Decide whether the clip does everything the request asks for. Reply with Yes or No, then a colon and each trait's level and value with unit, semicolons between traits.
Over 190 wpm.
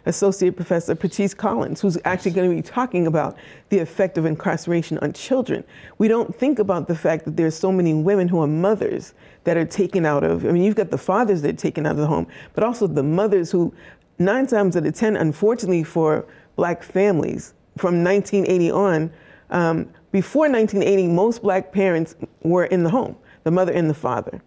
Yes: average, 200 wpm